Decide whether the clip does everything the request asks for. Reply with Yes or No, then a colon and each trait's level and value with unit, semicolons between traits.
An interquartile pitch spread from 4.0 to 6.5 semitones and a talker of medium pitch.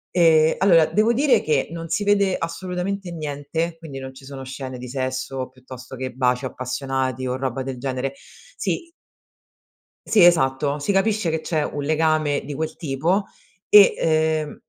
Yes: average, 4.4 semitones; medium, 150 Hz